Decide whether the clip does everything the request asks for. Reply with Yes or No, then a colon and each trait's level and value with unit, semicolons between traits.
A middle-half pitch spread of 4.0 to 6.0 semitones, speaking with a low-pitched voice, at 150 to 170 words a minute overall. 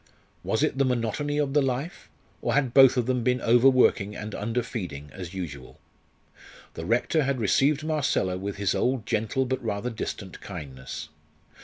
Yes: average, 5.2 semitones; low, 120 Hz; average, 160 wpm